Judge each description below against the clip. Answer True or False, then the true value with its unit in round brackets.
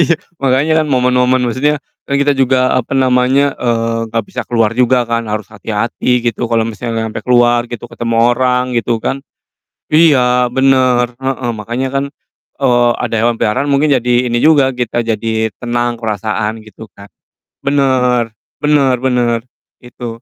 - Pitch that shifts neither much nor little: False (2.2 semitones)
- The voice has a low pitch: True (125 Hz)